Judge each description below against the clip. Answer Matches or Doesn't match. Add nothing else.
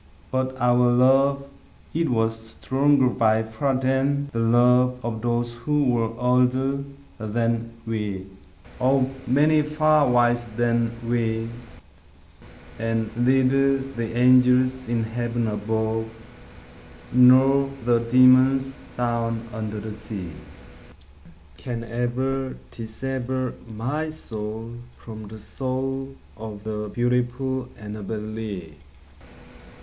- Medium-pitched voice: Doesn't match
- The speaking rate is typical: Doesn't match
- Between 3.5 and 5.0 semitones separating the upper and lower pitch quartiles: Doesn't match